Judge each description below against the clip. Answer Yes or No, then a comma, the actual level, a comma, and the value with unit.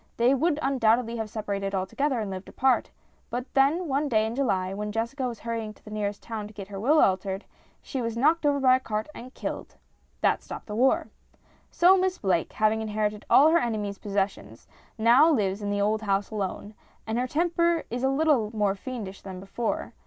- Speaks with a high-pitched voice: Yes, high, 225 Hz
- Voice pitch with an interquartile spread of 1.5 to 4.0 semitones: No, average, 4.7 semitones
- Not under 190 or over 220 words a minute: Yes, average, 200 wpm